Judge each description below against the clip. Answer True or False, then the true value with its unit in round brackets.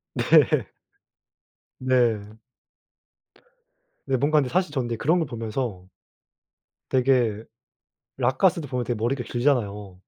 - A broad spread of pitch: False (3.5 semitones)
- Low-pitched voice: True (125 Hz)